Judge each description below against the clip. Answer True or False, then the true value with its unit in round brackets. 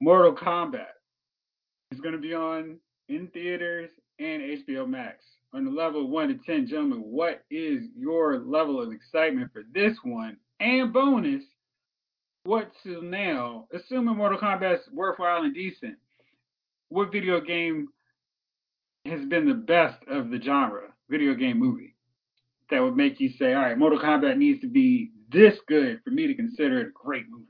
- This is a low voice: False (230 Hz)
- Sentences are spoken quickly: False (165 wpm)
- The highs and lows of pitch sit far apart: True (7.7 semitones)